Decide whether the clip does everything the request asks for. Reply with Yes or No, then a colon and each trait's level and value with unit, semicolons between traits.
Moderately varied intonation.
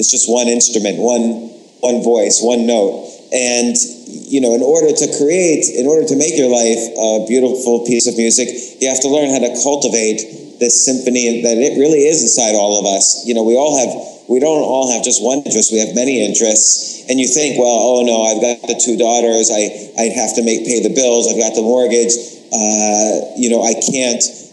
No: narrow, 1.7 semitones